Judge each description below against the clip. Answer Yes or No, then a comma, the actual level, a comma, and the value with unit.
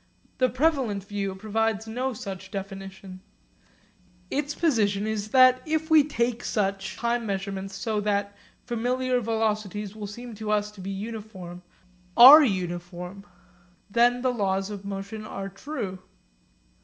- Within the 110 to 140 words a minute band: Yes, slow, 135 wpm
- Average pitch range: Yes, average, 3.7 semitones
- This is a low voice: No, high, 210 Hz